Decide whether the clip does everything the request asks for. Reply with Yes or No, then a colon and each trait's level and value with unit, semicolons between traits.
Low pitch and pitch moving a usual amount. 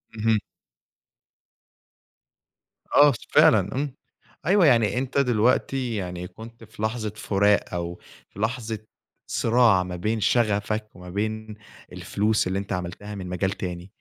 Yes: low, 110 Hz; average, 3.4 semitones